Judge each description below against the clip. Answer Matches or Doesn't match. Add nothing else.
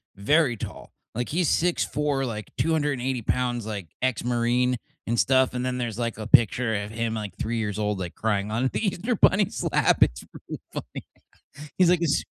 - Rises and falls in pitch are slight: Doesn't match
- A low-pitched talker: Matches